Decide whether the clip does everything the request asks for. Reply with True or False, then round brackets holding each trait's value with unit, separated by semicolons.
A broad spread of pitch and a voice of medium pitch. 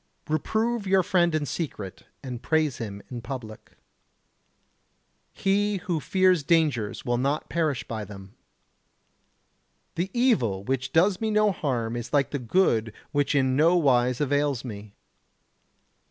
True (6.8 semitones; 145 Hz)